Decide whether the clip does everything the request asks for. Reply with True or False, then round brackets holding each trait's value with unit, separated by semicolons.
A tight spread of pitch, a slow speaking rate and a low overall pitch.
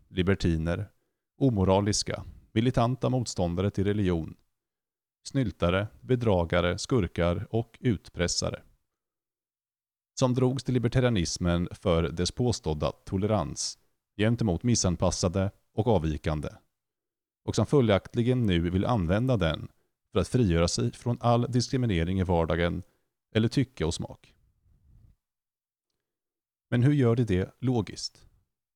False (5.5 semitones; 100 wpm; 105 Hz)